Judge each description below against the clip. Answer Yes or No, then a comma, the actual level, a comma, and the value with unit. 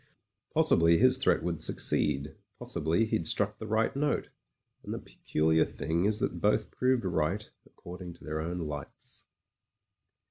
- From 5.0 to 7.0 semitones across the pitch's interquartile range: Yes, wide, 5.4 semitones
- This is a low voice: Yes, very low, 90 Hz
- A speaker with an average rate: Yes, average, 145 wpm